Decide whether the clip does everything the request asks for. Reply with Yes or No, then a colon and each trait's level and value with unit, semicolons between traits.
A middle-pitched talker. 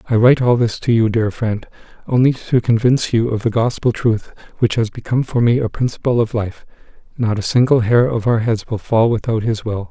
No: low, 115 Hz